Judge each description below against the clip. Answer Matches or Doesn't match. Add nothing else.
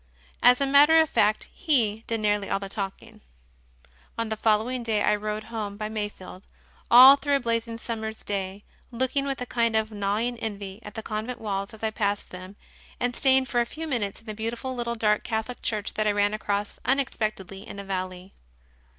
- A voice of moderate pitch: Doesn't match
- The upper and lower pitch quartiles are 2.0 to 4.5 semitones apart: Matches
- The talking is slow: Doesn't match